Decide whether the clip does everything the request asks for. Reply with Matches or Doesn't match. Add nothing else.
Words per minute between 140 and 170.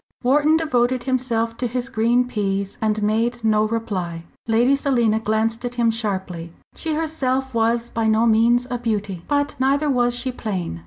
Matches